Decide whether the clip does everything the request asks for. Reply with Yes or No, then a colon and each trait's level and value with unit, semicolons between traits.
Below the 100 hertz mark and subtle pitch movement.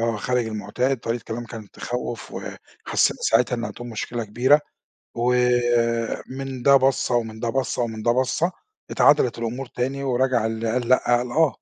No: low, 120 Hz; narrow, 1.9 semitones